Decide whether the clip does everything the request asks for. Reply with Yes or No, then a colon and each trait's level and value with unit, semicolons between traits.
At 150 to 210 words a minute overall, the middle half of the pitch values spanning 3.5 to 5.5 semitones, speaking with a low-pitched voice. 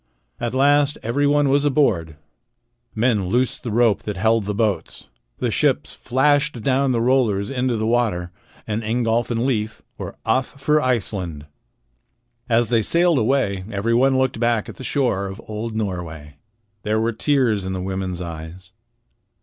Yes: average, 155 wpm; average, 4.8 semitones; low, 115 Hz